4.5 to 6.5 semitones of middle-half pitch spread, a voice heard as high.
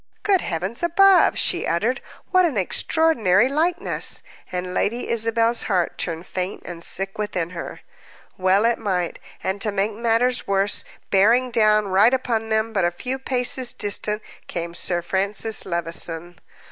Yes: average, 4.8 semitones; high, 210 Hz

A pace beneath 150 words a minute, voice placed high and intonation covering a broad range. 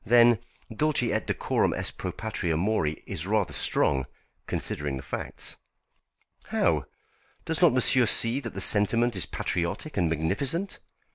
No: average, 140 wpm; low, 110 Hz; wide, 6.6 semitones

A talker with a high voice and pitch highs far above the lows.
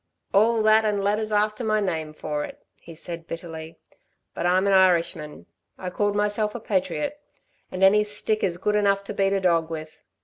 No: high, 195 Hz; average, 3.7 semitones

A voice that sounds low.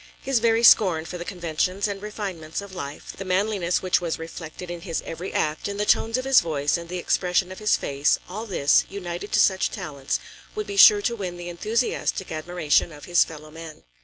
No: medium, 180 Hz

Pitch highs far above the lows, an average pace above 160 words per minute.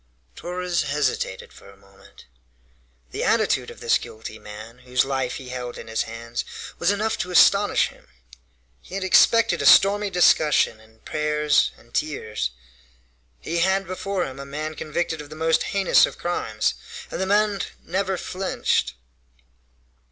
No: wide, 7.3 semitones; average, 150 wpm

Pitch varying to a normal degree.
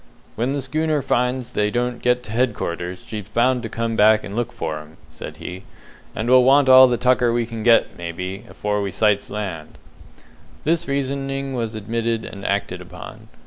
Yes: average, 3.9 semitones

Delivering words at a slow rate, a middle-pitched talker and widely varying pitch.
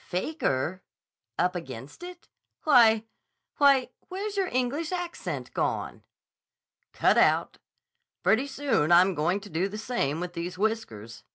No: slow, 120 wpm; high, 215 Hz; wide, 8.6 semitones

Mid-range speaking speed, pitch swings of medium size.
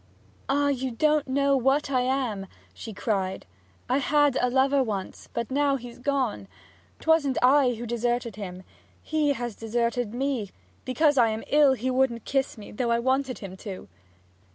Yes: average, 165 wpm; average, 3.3 semitones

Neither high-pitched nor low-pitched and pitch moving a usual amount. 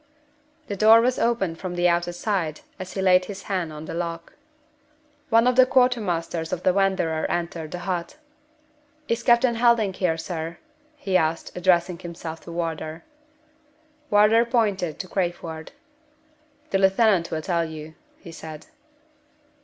Yes: medium, 180 Hz; average, 3.8 semitones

